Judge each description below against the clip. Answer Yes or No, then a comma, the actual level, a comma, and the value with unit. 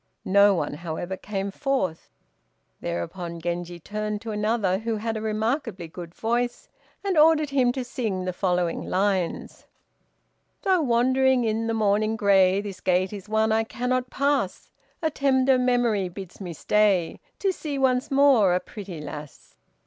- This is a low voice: No, high, 215 Hz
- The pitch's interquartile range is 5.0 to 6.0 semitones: Yes, average, 5.3 semitones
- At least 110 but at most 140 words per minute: No, average, 150 wpm